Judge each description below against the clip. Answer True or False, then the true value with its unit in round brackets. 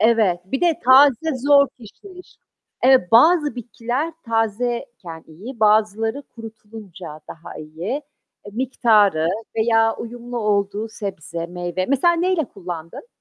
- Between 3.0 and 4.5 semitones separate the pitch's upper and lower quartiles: False (4.9 semitones)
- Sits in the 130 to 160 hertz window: False (225 Hz)